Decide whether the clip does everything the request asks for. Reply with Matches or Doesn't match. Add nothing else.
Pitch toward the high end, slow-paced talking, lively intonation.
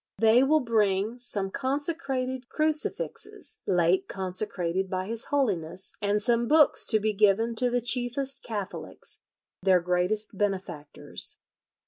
Doesn't match